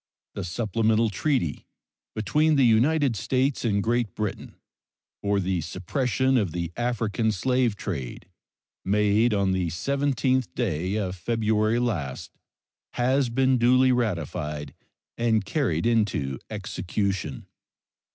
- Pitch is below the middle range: Yes, low, 110 Hz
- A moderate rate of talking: No, slow, 110 wpm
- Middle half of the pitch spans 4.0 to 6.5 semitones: Yes, average, 4.8 semitones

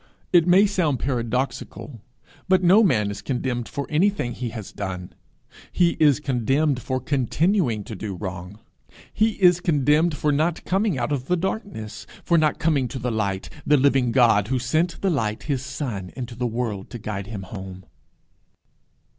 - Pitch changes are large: Yes, wide, 6.5 semitones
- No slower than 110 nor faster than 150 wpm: No, average, 170 wpm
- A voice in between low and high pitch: No, low, 130 Hz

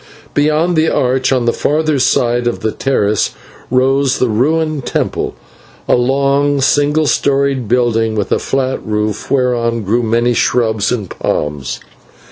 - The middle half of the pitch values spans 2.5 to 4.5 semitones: Yes, average, 3.4 semitones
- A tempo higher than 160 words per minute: No, average, 140 wpm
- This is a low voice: Yes, low, 125 Hz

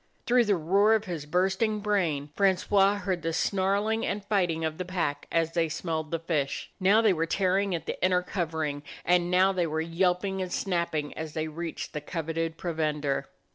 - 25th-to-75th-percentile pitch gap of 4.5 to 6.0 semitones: No, average, 3.3 semitones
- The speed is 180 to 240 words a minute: Yes, average, 185 wpm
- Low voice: No, medium, 175 Hz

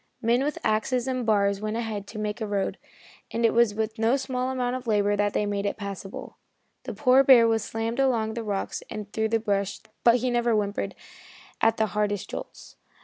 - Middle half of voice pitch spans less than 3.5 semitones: Yes, average, 2.7 semitones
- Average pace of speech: No, fast, 215 wpm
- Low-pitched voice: No, high, 220 Hz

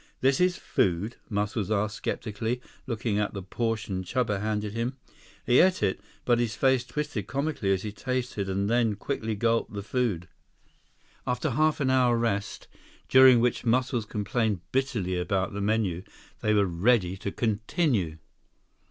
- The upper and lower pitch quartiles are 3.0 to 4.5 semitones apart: Yes, average, 3.7 semitones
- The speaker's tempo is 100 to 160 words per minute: Yes, average, 155 wpm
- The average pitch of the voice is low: Yes, low, 110 Hz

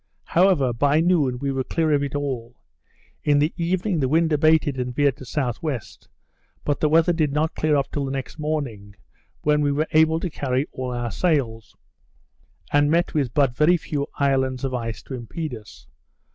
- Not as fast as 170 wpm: No, average, 185 wpm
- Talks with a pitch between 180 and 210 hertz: No, medium, 145 Hz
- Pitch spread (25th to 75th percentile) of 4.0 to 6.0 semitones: No, average, 3.4 semitones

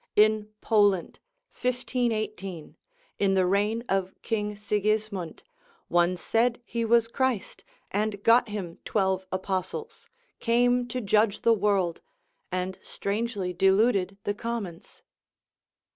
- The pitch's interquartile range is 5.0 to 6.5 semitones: No, average, 3.3 semitones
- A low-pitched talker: No, high, 210 Hz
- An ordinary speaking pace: No, slow, 110 wpm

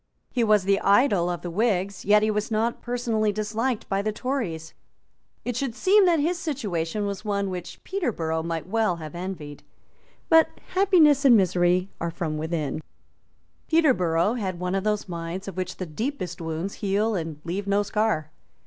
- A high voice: Yes, high, 200 Hz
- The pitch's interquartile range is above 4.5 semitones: Yes, average, 5.1 semitones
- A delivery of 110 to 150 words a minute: No, average, 170 wpm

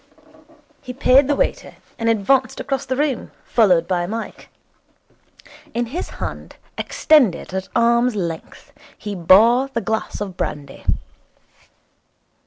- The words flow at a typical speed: No, slow, 120 wpm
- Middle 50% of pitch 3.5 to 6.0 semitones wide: Yes, wide, 5.5 semitones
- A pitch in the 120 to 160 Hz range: No, high, 230 Hz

